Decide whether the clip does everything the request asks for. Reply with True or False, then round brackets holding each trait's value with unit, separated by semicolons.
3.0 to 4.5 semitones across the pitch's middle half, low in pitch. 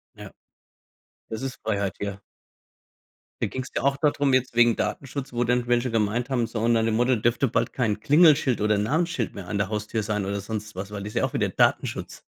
True (3.5 semitones; 115 Hz)